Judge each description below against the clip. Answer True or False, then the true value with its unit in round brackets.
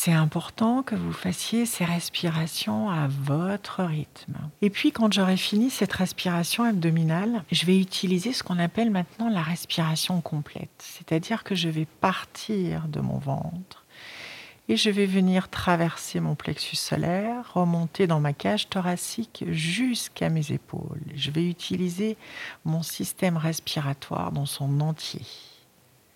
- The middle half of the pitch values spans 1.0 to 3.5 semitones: False (4.0 semitones)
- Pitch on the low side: False (175 Hz)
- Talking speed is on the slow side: True (140 wpm)